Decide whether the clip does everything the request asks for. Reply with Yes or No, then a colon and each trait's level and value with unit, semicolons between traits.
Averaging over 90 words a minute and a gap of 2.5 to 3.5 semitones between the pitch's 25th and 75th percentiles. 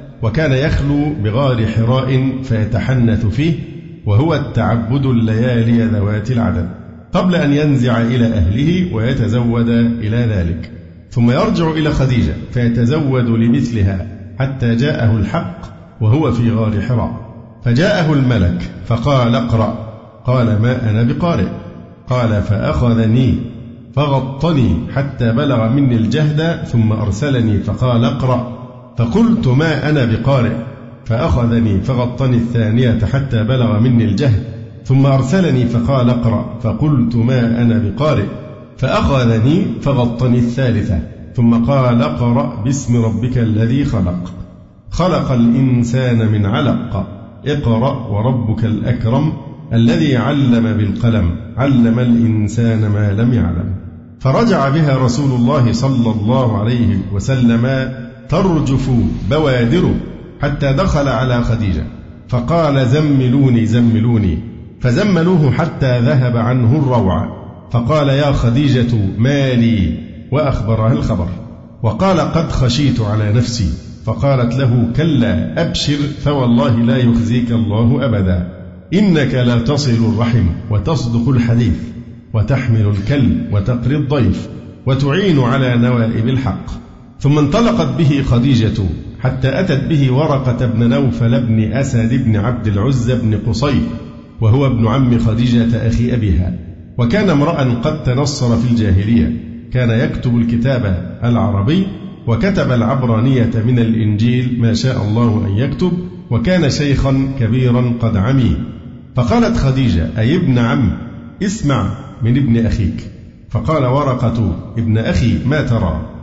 Yes: average, 110 wpm; average, 2.9 semitones